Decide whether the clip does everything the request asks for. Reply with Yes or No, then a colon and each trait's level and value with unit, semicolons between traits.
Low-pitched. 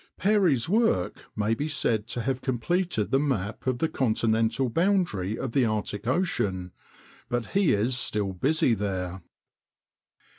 Yes: low, 120 Hz